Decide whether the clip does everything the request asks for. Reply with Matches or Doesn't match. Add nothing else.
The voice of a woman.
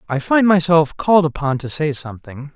Doesn't match